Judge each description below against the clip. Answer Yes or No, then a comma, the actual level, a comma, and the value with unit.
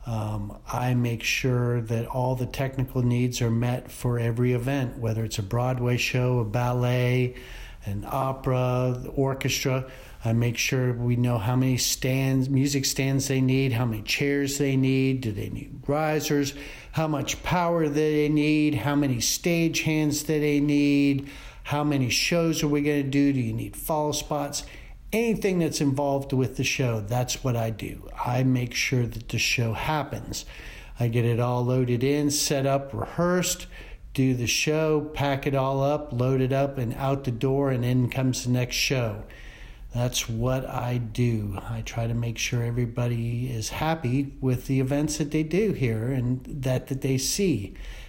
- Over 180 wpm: No, average, 175 wpm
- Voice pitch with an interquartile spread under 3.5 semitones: Yes, average, 2.8 semitones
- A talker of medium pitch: No, low, 130 Hz